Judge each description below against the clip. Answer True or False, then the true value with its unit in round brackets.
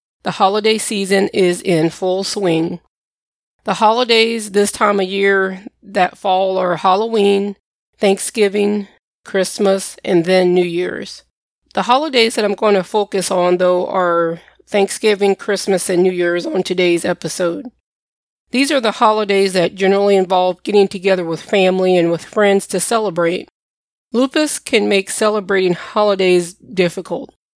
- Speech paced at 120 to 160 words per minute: True (135 wpm)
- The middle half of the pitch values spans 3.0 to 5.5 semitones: False (2.4 semitones)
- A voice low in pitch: False (195 Hz)